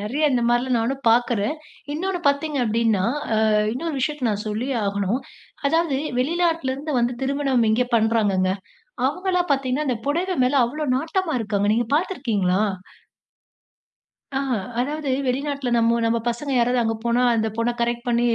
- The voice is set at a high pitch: Yes, very high, 250 Hz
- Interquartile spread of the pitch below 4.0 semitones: No, average, 4.3 semitones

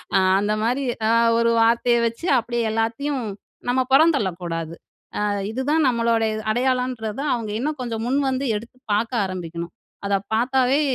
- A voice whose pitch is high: Yes, high, 235 Hz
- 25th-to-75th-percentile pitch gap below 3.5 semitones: Yes, average, 3.1 semitones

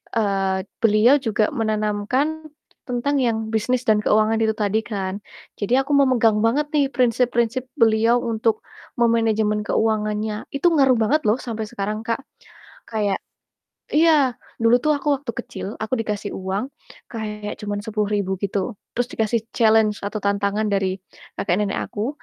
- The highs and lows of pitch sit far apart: No, narrow, 2.6 semitones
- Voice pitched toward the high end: Yes, high, 220 Hz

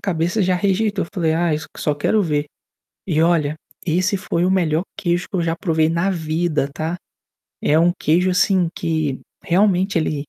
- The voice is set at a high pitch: No, medium, 170 Hz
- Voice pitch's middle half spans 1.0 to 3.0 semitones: Yes, average, 2.7 semitones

